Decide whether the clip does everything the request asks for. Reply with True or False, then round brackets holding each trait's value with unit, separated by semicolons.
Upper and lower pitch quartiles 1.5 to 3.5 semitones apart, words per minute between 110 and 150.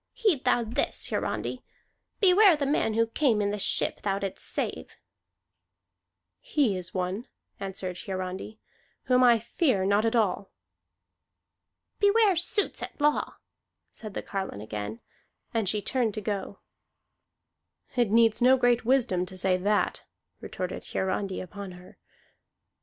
False (5.0 semitones; 135 wpm)